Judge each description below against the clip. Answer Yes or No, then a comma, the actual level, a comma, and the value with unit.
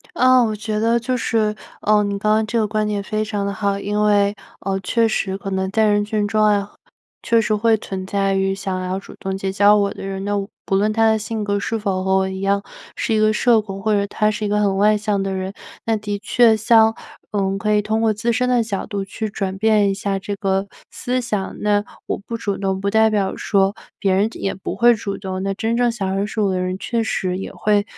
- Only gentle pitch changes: Yes, narrow, 1.9 semitones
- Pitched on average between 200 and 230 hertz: Yes, high, 205 Hz